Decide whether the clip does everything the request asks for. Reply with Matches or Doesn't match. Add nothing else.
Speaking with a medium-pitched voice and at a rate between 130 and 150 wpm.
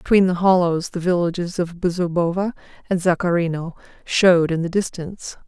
Matches